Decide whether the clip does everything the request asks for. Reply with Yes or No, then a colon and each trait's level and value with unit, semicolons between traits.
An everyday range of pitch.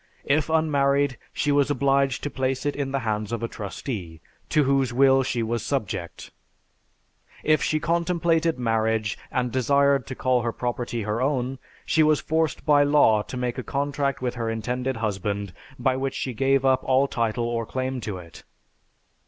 Yes: average, 3.4 semitones